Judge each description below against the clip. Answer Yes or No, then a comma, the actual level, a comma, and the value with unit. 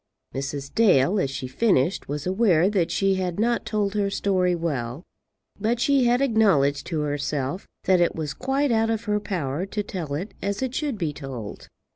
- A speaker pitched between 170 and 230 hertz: Yes, medium, 185 Hz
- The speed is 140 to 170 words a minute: No, average, 185 wpm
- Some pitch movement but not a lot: No, wide, 6.9 semitones